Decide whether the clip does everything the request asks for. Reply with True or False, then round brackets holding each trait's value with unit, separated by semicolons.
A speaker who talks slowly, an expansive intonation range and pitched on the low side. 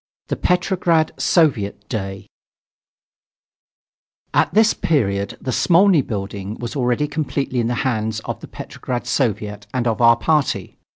True (130 wpm; 6.3 semitones; 120 Hz)